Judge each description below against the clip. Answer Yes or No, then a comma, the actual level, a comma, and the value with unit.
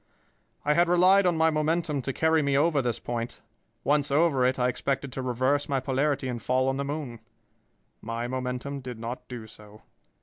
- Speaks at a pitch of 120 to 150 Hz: Yes, low, 135 Hz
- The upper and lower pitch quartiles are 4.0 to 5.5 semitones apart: No, average, 3.2 semitones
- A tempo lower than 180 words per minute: No, average, 190 wpm